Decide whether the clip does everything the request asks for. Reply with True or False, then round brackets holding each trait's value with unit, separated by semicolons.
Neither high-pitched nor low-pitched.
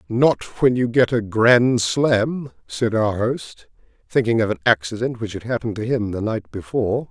False (115 Hz)